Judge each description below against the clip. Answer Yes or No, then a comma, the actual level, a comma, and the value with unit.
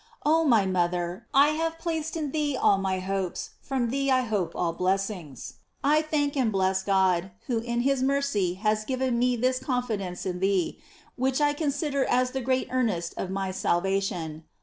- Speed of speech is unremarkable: Yes, average, 180 wpm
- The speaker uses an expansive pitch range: Yes, wide, 6.4 semitones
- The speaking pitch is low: No, high, 235 Hz